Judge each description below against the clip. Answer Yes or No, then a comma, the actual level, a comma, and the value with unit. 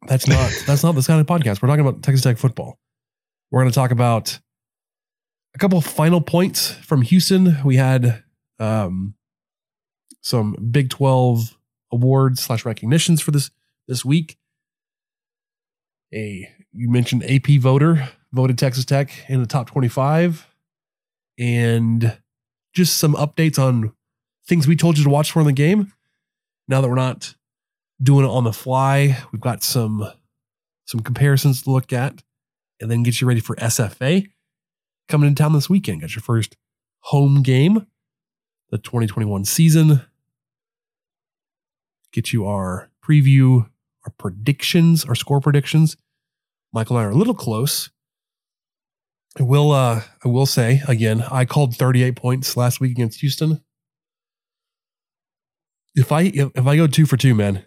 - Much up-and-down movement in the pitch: No, average, 4.1 semitones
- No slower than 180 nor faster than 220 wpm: No, average, 150 wpm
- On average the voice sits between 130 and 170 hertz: Yes, low, 135 Hz